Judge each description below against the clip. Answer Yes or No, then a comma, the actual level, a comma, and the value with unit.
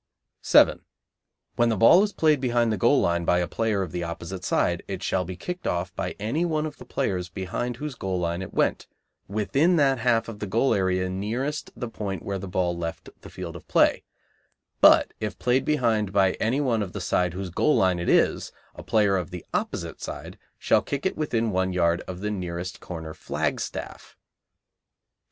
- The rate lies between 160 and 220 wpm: Yes, average, 200 wpm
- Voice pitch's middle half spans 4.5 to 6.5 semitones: Yes, average, 5.2 semitones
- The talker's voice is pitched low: Yes, low, 100 Hz